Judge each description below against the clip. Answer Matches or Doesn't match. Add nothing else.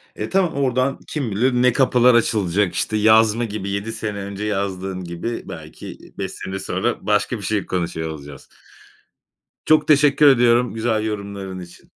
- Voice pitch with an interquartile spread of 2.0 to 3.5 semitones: Doesn't match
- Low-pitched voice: Matches